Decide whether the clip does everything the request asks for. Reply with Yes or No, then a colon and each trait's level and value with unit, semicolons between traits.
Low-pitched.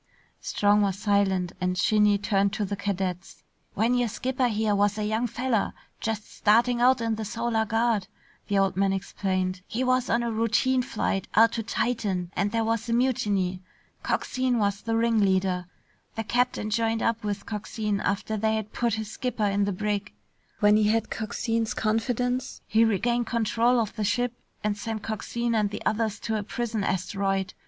No: high, 215 Hz